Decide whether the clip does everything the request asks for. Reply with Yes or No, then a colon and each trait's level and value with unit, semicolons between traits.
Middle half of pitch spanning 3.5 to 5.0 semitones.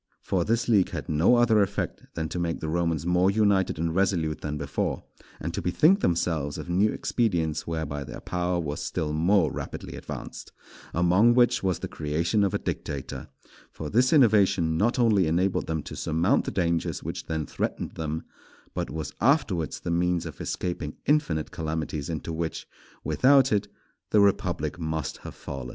Yes: average, 4.2 semitones